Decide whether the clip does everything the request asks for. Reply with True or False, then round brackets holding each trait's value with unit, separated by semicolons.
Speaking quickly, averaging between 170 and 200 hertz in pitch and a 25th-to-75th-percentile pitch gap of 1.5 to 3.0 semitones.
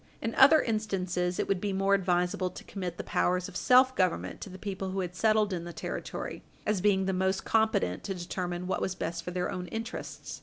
True (220 wpm; 190 Hz; 2.6 semitones)